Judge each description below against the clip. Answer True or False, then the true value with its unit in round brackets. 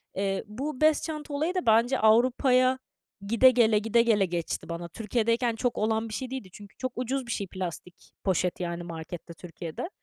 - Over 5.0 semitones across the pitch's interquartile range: True (5.5 semitones)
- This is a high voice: True (225 Hz)